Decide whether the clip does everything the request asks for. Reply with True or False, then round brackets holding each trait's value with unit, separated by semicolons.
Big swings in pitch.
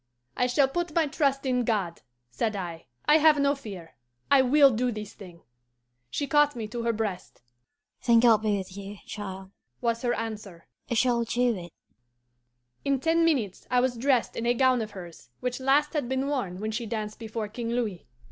False (4.4 semitones)